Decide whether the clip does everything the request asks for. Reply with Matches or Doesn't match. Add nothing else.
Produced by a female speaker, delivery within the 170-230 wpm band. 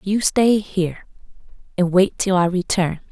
Doesn't match